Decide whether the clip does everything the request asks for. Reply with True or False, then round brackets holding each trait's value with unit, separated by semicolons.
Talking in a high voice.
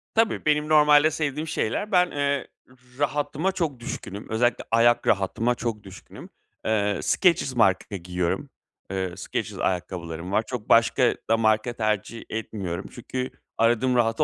False (115 Hz)